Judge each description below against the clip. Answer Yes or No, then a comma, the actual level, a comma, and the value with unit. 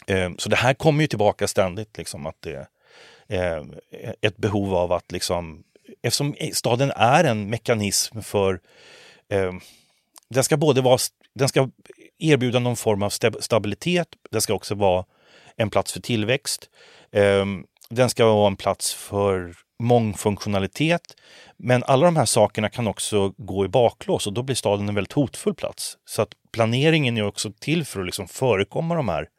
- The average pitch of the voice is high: No, low, 110 Hz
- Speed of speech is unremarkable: Yes, average, 165 wpm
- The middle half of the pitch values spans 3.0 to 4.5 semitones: No, average, 5.1 semitones